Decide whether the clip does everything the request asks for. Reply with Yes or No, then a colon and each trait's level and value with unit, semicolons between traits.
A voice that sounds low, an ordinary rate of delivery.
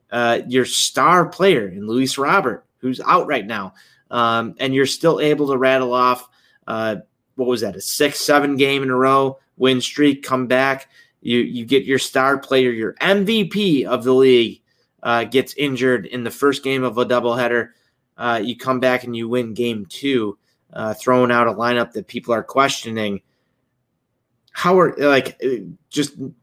Yes: low, 130 Hz; average, 175 wpm